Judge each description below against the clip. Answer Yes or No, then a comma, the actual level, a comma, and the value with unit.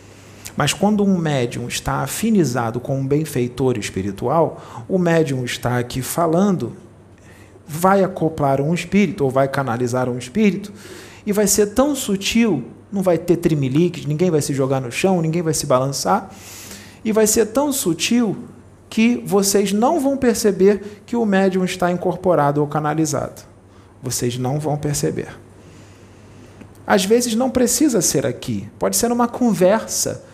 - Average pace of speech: Yes, average, 145 wpm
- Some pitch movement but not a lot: No, wide, 8.3 semitones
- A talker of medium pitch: Yes, medium, 160 Hz